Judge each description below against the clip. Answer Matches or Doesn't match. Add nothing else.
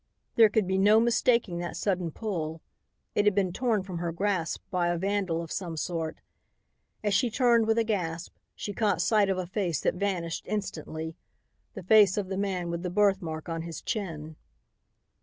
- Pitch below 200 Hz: Matches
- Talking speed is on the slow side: Doesn't match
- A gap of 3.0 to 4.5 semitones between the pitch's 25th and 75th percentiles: Matches